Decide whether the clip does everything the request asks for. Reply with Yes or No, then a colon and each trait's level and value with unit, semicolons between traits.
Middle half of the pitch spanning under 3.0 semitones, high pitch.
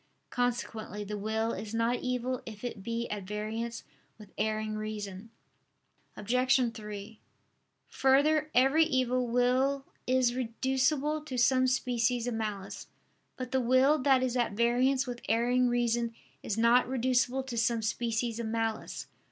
Yes: narrow, 2.5 semitones; high, 240 Hz